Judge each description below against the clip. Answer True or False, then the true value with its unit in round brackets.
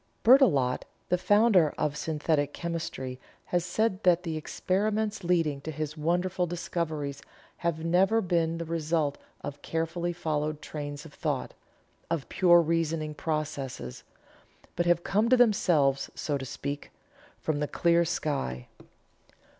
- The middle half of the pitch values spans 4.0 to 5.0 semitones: False (3.0 semitones)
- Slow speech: True (130 wpm)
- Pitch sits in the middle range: True (165 Hz)